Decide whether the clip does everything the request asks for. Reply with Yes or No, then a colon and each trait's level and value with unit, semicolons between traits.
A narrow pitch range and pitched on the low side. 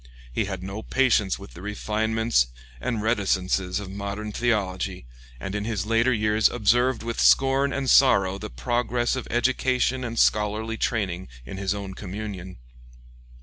No: average, 3.6 semitones; low, 105 Hz